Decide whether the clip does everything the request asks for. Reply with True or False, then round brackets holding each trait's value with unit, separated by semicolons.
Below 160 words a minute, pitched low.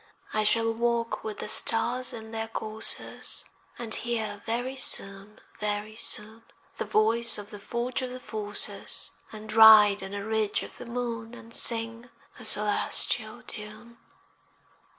False (145 wpm; 220 Hz)